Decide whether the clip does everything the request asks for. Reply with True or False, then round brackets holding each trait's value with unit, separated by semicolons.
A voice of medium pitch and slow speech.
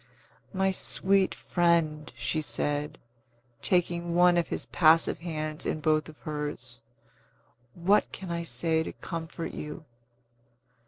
True (165 Hz; 120 wpm)